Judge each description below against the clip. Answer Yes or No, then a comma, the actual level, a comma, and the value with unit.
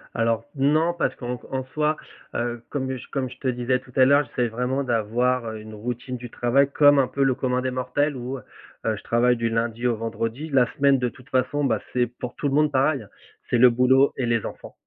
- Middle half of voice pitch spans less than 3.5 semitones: Yes, narrow, 2.4 semitones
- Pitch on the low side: Yes, low, 125 Hz